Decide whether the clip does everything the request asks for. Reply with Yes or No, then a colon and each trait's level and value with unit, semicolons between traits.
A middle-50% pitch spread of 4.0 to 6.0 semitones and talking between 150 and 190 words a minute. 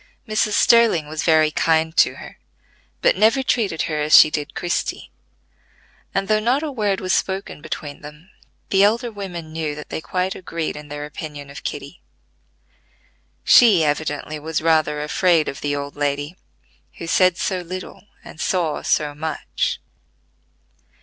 Yes: average, 4.3 semitones; average, 155 wpm